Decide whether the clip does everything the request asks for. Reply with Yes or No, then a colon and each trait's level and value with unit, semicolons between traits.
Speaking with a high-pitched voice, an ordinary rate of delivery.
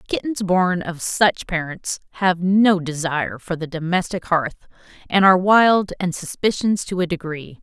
No: medium, 175 Hz; average, 155 wpm